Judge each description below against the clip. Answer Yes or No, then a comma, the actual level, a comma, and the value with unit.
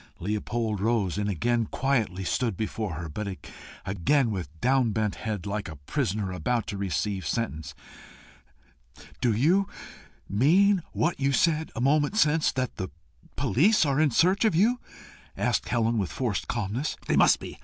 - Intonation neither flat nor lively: No, wide, 6.3 semitones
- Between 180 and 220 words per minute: No, average, 155 wpm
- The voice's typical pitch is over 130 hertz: No, low, 115 Hz